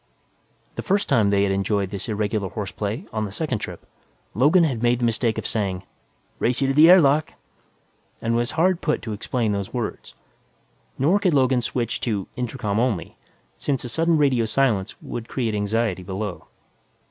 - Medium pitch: No, low, 115 Hz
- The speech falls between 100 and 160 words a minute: No, average, 175 wpm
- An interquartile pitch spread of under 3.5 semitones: No, average, 4.8 semitones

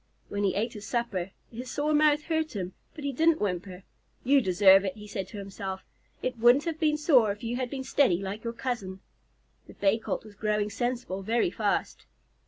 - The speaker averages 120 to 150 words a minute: No, average, 200 wpm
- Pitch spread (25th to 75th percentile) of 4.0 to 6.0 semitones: Yes, average, 5.0 semitones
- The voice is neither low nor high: No, high, 225 Hz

